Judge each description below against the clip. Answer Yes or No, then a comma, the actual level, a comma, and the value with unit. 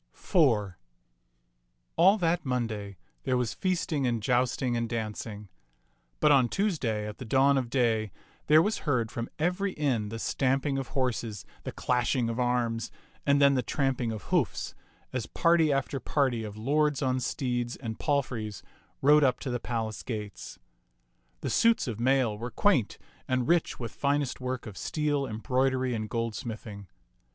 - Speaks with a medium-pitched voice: No, low, 125 Hz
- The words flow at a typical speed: Yes, average, 155 wpm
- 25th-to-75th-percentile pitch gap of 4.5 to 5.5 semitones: No, average, 3.8 semitones